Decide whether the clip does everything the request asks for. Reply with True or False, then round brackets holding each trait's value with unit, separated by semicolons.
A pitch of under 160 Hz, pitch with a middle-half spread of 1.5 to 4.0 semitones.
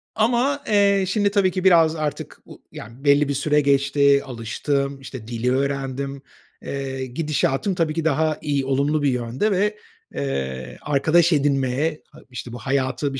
True (140 Hz; 3.5 semitones)